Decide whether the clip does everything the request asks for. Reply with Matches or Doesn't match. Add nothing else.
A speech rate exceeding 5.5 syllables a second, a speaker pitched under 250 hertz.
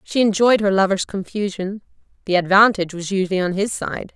Matches